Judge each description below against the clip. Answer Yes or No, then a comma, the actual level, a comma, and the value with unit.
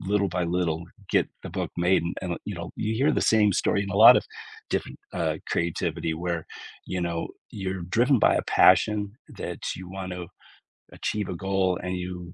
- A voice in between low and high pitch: No, very low, 90 Hz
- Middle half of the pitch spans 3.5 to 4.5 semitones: No, narrow, 2.6 semitones